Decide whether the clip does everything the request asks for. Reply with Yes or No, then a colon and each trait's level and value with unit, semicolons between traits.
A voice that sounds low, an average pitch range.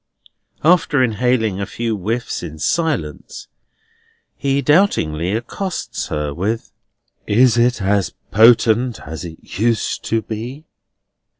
Yes: low, 115 Hz; average, 4.7 semitones